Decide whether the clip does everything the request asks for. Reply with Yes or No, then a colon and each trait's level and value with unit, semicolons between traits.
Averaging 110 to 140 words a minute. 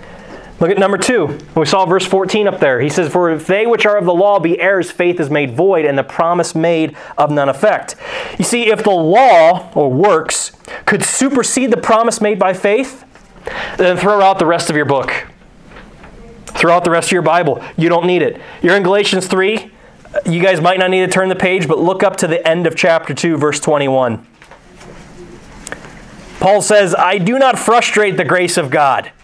No: fast, 205 wpm